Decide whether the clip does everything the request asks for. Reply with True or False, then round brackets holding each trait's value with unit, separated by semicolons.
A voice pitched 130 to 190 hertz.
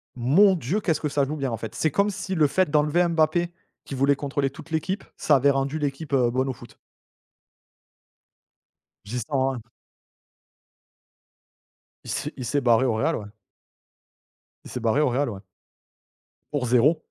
True (140 Hz)